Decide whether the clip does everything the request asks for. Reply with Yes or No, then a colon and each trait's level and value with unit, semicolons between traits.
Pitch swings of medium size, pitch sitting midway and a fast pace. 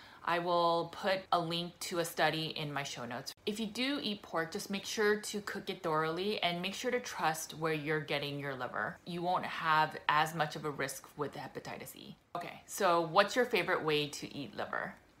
Yes: average, 4.3 semitones; medium, 170 Hz; fast, 215 wpm